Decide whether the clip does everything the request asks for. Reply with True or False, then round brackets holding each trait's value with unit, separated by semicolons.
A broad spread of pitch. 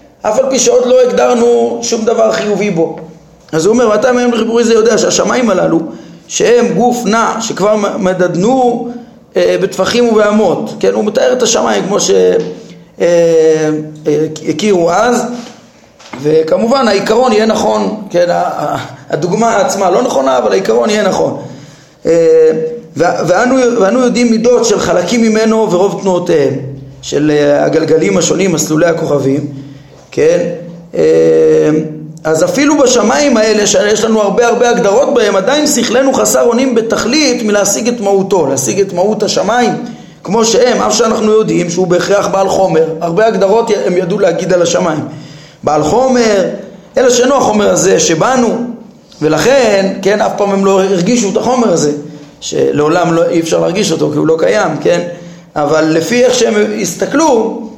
True (5.8 semitones)